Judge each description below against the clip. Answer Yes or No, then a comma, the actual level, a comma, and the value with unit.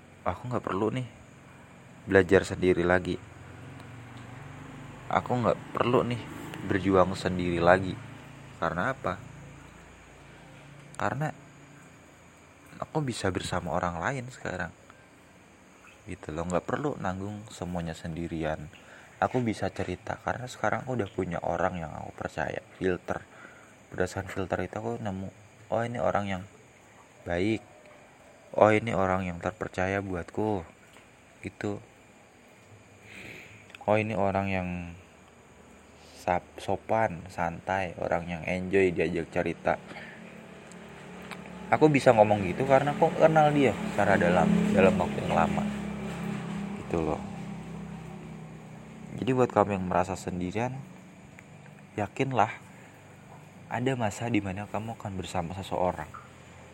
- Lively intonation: Yes, wide, 6.0 semitones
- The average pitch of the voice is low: Yes, low, 105 Hz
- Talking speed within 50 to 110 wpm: Yes, average, 105 wpm